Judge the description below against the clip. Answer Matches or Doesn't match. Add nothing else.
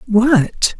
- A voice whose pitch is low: Doesn't match